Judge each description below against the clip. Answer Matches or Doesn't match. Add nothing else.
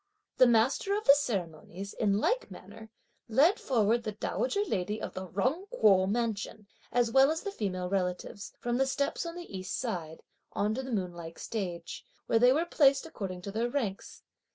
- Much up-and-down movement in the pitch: Matches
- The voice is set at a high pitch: Matches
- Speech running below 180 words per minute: Doesn't match